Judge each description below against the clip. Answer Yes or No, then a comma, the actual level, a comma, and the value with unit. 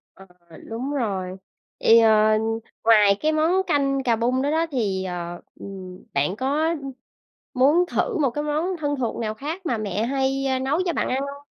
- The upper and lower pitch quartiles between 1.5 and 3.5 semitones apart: No, average, 5.2 semitones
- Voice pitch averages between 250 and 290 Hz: Yes, very high, 260 Hz